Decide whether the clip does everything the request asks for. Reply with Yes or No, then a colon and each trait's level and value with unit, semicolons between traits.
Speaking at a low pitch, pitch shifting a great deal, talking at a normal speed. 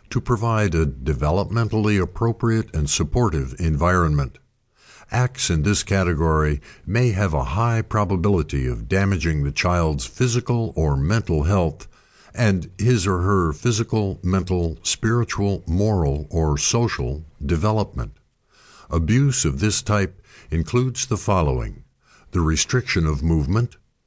No: very low, 95 Hz; wide, 5.8 semitones; slow, 115 wpm